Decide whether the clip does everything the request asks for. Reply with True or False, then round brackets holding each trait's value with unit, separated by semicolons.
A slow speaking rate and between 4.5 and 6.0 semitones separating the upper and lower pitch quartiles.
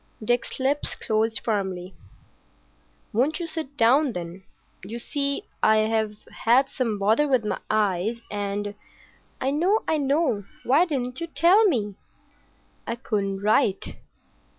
True (130 wpm; 5.4 semitones)